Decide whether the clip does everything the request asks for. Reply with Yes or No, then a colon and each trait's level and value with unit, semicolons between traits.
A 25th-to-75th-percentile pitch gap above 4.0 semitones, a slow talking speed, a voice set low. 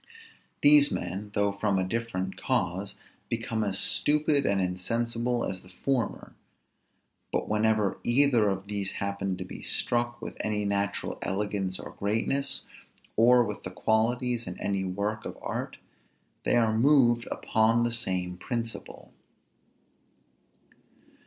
No: average, 3.4 semitones; slow, 130 wpm; low, 110 Hz